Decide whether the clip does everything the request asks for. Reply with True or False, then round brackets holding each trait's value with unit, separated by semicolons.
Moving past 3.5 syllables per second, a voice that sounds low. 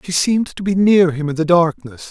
False (5.5 syllables/s; 170 Hz)